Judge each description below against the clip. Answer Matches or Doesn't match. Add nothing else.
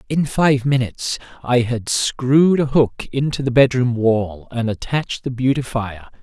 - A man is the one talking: Matches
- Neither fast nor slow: Matches